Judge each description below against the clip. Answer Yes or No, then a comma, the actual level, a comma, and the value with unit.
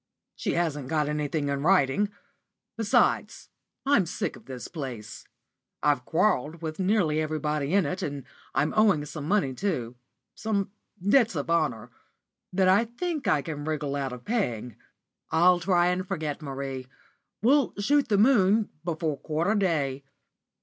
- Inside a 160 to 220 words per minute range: No, average, 150 wpm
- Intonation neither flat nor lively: No, wide, 5.7 semitones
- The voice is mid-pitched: Yes, medium, 160 Hz